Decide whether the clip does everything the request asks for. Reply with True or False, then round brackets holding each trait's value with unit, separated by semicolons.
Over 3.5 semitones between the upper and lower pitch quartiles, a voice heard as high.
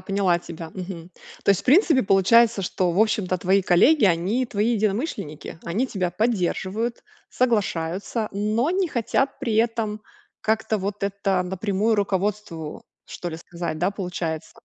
True (3.9 semitones; 200 Hz)